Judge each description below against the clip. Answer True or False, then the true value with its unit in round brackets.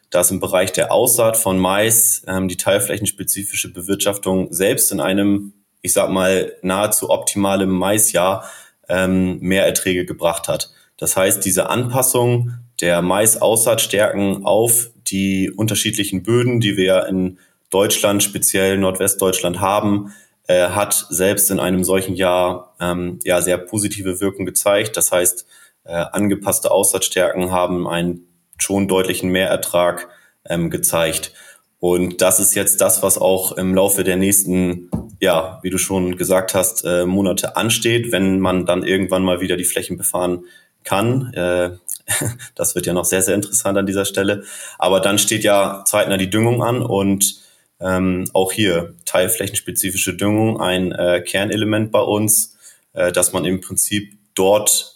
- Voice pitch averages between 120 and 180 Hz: False (95 Hz)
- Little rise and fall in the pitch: True (1.9 semitones)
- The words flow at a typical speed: True (145 wpm)